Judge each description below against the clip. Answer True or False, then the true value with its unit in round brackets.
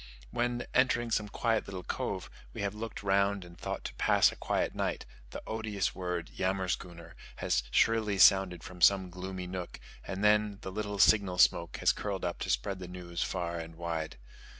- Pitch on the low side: True (95 Hz)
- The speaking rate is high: False (180 wpm)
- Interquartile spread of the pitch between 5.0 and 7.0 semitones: False (2.8 semitones)